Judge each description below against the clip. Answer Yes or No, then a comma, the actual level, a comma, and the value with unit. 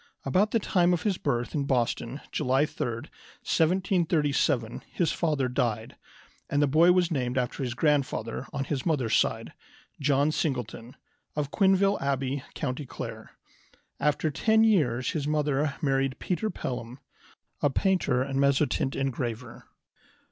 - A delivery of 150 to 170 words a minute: No, slow, 135 wpm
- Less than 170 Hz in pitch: Yes, medium, 140 Hz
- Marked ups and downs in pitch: No, average, 4.0 semitones